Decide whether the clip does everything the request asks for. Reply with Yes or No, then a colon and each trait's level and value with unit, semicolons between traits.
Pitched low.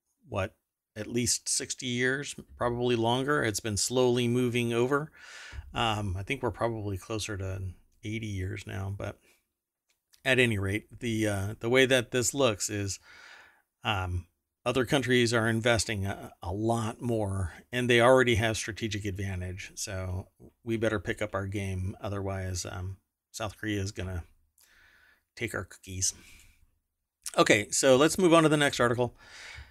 Yes: low, 110 Hz